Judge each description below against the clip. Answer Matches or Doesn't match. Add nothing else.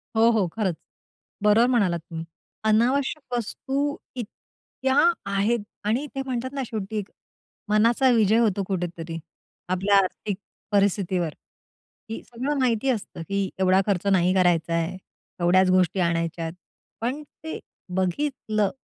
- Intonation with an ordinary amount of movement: Matches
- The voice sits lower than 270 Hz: Matches